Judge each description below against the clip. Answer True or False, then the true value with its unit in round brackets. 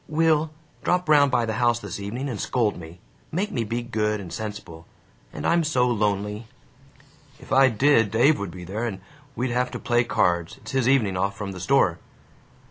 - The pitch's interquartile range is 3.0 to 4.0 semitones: False (4.8 semitones)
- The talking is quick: False (195 wpm)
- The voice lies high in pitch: False (115 Hz)